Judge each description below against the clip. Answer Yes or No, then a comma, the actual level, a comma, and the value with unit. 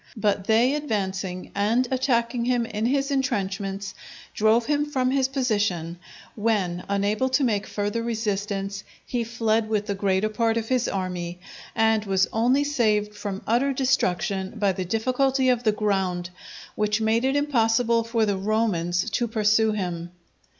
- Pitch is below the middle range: No, high, 220 Hz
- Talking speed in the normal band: Yes, average, 150 wpm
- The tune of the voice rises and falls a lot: No, average, 3.5 semitones